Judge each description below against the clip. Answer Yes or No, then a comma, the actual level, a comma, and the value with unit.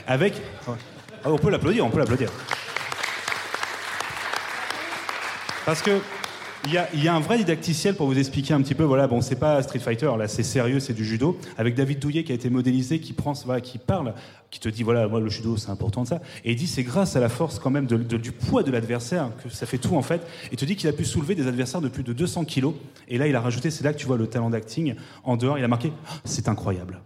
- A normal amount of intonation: Yes, average, 4.5 semitones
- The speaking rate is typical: No, fast, 255 wpm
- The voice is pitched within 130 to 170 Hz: Yes, low, 135 Hz